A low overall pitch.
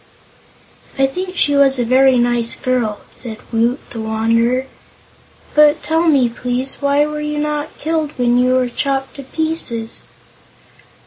No: very high, 265 Hz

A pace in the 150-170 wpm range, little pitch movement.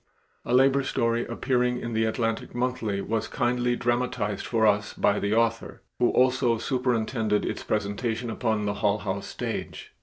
Yes: average, 155 wpm; narrow, 2.3 semitones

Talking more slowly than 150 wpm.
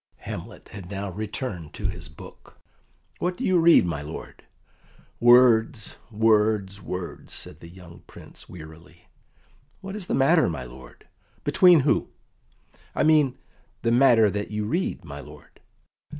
Yes: average, 140 wpm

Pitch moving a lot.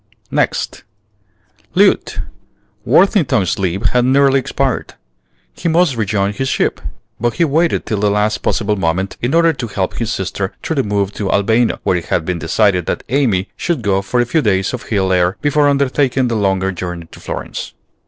Yes: wide, 5.8 semitones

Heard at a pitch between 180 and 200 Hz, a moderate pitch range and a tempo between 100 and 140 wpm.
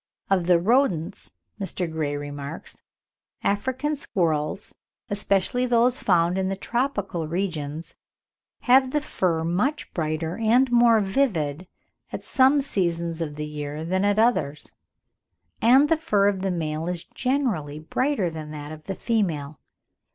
No: medium, 185 Hz; wide, 7.1 semitones; slow, 135 wpm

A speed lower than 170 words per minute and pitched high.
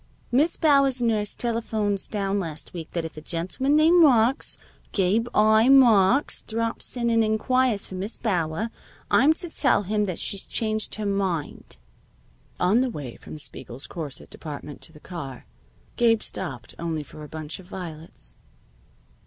Yes: average, 155 wpm; high, 205 Hz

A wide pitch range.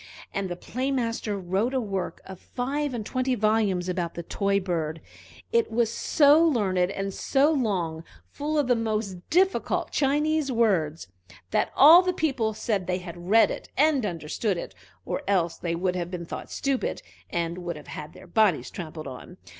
Yes: wide, 6.7 semitones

